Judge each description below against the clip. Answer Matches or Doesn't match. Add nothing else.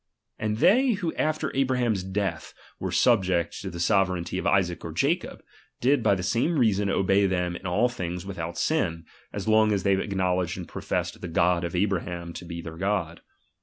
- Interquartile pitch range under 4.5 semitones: Matches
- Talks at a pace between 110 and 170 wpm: Doesn't match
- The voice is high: Doesn't match